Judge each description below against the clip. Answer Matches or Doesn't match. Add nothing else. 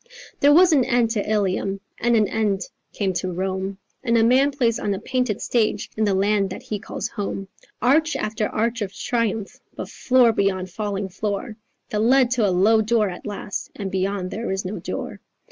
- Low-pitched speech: Doesn't match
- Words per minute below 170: Doesn't match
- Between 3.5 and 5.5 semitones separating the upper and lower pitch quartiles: Doesn't match